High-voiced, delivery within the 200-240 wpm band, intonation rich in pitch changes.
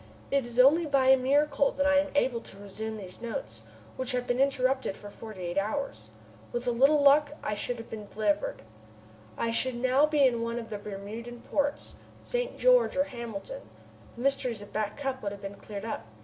No: high, 245 Hz; fast, 205 wpm; average, 4.7 semitones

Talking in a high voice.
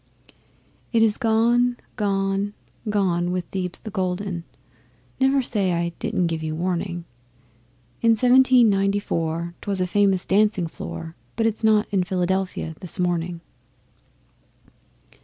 Yes: high, 195 Hz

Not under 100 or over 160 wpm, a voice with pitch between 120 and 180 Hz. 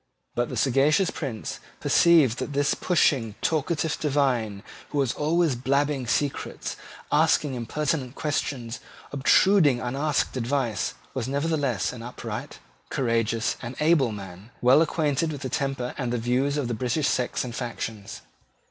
Yes: slow, 135 wpm; low, 135 Hz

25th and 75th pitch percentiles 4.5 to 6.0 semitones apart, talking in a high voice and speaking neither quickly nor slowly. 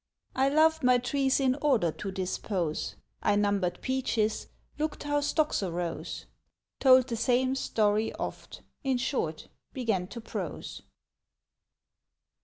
No: average, 4.9 semitones; high, 245 Hz; slow, 120 wpm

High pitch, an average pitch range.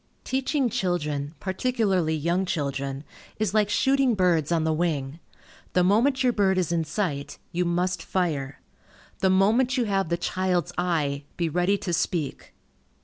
No: medium, 180 Hz; average, 4.1 semitones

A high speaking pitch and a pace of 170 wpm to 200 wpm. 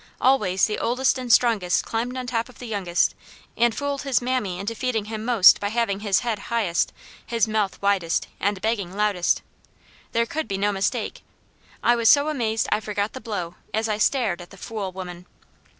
Yes: high, 220 Hz; average, 190 wpm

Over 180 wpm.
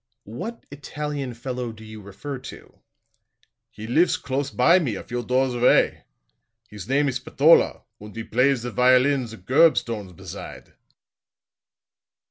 No: average, 140 wpm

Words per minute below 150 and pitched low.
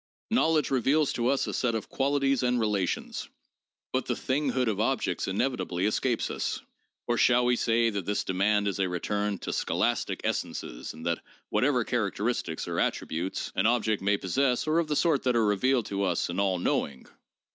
No: average, 185 wpm; low, 115 Hz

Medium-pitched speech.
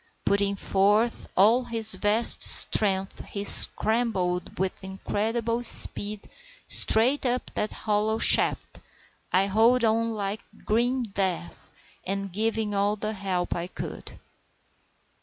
No: high, 210 Hz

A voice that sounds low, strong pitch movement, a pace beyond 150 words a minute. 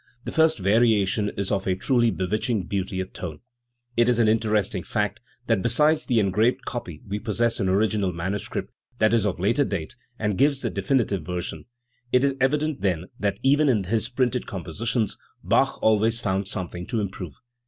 No: low, 105 Hz; average, 3.8 semitones; average, 175 wpm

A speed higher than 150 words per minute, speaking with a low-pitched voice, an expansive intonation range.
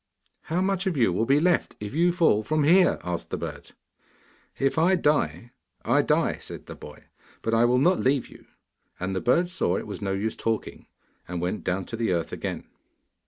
Yes: fast, 205 wpm; low, 125 Hz; wide, 8.8 semitones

